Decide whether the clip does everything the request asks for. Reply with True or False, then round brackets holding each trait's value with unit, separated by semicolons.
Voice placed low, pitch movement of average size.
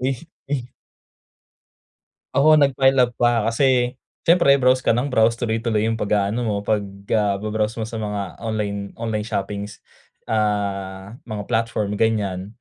True (110 Hz; 3.0 semitones)